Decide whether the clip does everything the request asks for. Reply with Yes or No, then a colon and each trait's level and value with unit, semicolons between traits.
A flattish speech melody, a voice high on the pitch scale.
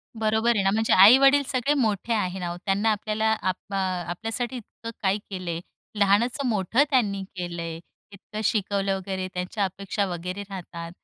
No: average, 3.2 semitones; high, 200 Hz